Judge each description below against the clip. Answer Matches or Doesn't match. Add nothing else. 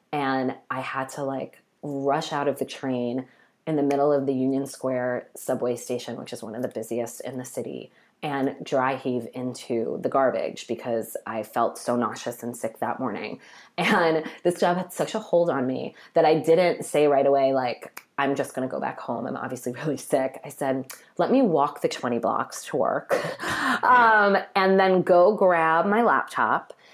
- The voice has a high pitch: Doesn't match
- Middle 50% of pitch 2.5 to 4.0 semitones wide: Doesn't match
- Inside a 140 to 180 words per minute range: Doesn't match